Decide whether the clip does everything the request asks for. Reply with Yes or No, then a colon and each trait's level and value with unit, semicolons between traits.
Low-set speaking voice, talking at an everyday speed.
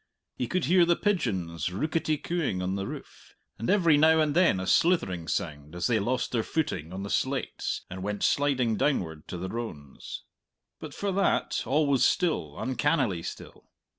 Yes: low, 120 Hz; average, 175 wpm